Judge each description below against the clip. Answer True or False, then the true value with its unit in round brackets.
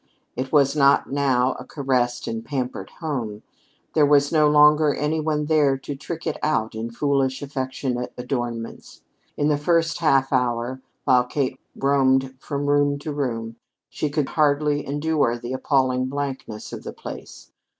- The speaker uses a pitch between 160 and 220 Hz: False (140 Hz)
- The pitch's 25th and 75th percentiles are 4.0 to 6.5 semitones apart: False (2.6 semitones)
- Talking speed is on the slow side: False (155 wpm)